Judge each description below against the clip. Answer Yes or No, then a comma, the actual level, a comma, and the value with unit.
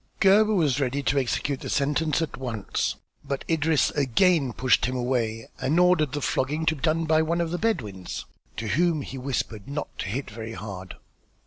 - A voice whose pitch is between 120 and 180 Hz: Yes, medium, 140 Hz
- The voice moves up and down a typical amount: Yes, average, 4.6 semitones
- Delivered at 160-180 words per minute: No, average, 190 wpm